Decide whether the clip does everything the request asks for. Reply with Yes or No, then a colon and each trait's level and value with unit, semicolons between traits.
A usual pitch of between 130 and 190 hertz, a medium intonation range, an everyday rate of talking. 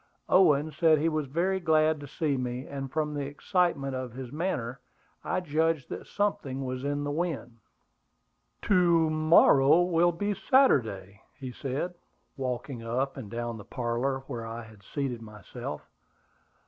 Yes: medium, 140 Hz; average, 4.6 semitones; average, 150 wpm